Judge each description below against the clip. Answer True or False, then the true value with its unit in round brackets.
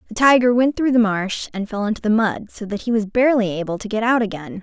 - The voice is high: True (220 Hz)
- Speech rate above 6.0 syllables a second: True (6.2 syllables/s)